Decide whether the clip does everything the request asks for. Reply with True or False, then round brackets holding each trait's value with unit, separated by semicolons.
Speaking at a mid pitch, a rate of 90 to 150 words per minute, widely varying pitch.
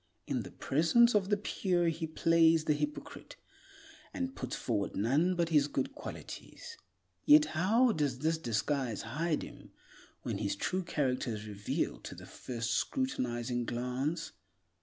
True (155 Hz; 145 wpm; 6.8 semitones)